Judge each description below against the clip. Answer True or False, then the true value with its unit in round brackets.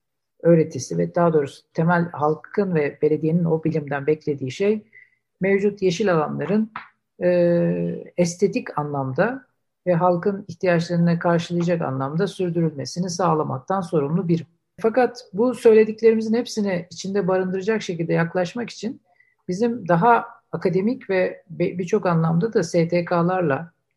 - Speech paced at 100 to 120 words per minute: True (110 wpm)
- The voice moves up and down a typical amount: True (4.1 semitones)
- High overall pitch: False (180 Hz)